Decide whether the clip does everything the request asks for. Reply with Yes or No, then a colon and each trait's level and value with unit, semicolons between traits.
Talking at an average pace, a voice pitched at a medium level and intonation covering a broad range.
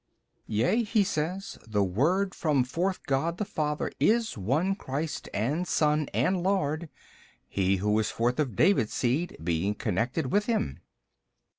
Yes: average, 150 wpm; medium, 150 Hz; wide, 8.6 semitones